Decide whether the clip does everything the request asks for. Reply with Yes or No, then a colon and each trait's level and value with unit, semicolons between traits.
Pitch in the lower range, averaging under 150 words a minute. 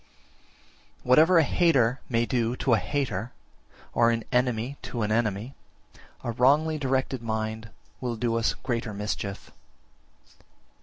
Yes: low, 120 Hz; slow, 135 wpm